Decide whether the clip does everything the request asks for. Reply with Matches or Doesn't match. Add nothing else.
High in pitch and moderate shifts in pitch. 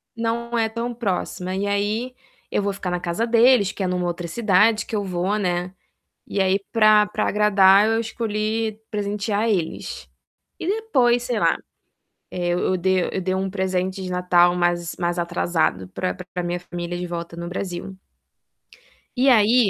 Matches